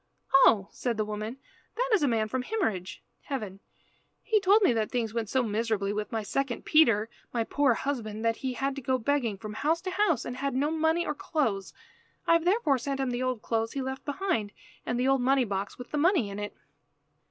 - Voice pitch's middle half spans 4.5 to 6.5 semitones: Yes, average, 4.8 semitones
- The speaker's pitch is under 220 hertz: No, very high, 250 Hz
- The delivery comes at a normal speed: No, fast, 220 wpm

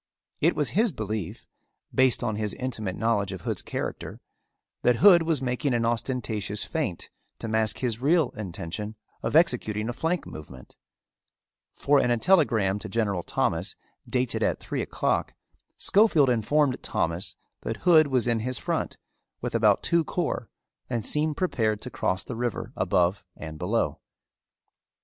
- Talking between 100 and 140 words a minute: No, average, 150 wpm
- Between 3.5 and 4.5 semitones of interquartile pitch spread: No, average, 5.3 semitones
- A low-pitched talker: Yes, low, 120 Hz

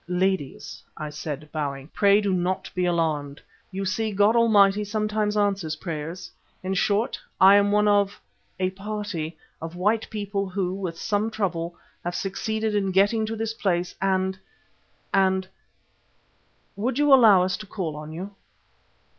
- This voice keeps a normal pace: Yes, average, 150 wpm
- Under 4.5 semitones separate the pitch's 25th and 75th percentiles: Yes, average, 3.0 semitones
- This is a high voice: Yes, high, 195 Hz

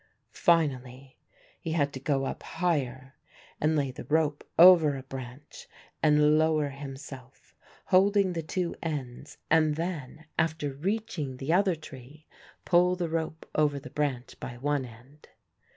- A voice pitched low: No, medium, 150 Hz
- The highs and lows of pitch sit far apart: No, average, 3.5 semitones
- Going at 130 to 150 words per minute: Yes, average, 140 wpm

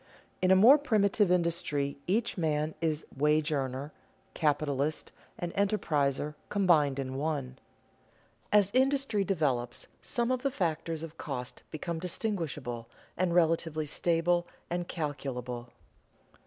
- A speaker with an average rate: No, slow, 120 wpm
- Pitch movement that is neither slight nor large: Yes, average, 4.4 semitones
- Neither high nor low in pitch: Yes, medium, 160 Hz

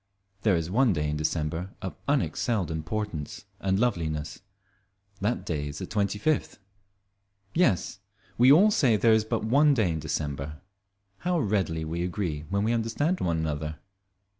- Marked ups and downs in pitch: Yes, wide, 6.7 semitones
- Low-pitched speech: Yes, very low, 95 Hz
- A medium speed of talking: Yes, average, 155 wpm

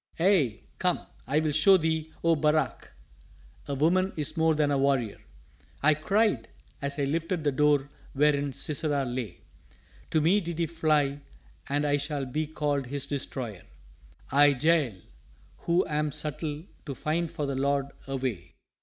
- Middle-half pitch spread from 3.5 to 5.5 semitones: No, narrow, 2.5 semitones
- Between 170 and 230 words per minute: No, average, 155 wpm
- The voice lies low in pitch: No, medium, 150 Hz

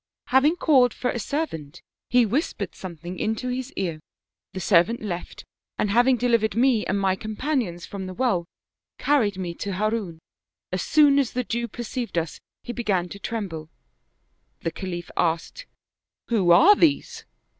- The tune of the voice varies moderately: No, wide, 5.7 semitones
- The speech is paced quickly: No, average, 155 wpm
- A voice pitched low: No, high, 215 Hz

